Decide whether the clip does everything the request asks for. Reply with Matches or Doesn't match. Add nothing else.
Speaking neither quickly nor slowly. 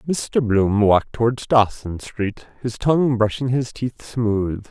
Matches